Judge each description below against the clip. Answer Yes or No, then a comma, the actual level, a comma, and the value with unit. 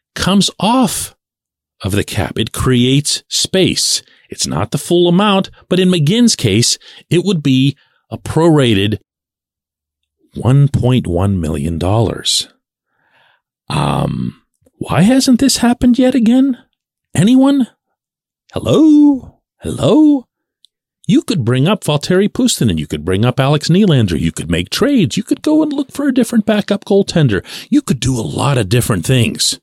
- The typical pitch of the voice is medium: Yes, medium, 155 Hz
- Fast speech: No, average, 140 wpm